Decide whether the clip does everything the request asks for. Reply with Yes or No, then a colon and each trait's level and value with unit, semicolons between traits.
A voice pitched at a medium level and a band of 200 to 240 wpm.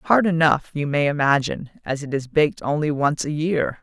Yes: medium, 150 Hz; fast, 205 wpm